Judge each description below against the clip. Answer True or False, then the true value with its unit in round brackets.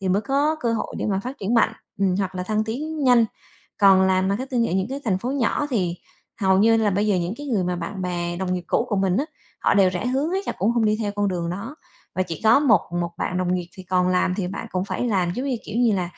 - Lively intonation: False (4.4 semitones)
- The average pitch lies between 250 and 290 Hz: False (200 Hz)